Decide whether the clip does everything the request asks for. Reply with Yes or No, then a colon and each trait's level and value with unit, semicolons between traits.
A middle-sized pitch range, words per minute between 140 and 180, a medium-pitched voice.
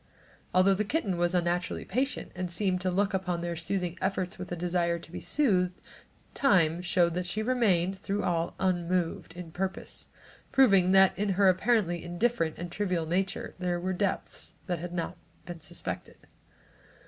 No: narrow, 1.9 semitones; average, 165 wpm; medium, 180 Hz